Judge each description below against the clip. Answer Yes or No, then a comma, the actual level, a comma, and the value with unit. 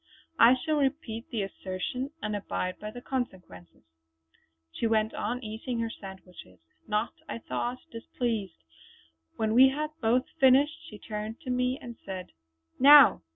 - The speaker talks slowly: No, average, 145 wpm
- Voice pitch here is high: Yes, high, 230 Hz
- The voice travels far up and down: No, average, 3.4 semitones